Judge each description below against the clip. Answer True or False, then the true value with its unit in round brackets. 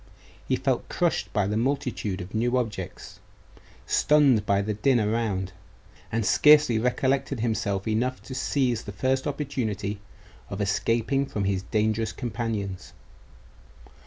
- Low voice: True (110 Hz)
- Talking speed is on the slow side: True (130 wpm)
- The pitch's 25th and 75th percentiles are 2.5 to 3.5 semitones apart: False (4.0 semitones)